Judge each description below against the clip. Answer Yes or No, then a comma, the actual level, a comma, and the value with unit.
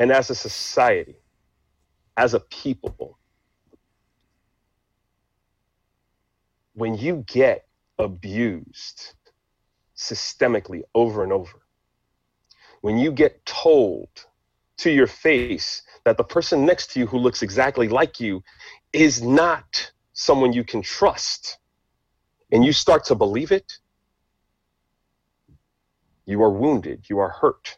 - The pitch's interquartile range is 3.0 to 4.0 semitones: No, average, 5.2 semitones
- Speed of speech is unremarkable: No, slow, 110 wpm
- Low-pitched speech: Yes, low, 115 Hz